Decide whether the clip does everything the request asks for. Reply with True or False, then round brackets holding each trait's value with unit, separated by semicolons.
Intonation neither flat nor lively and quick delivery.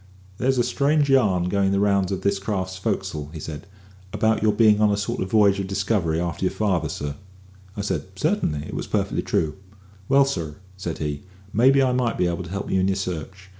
True (3.4 semitones; 220 wpm)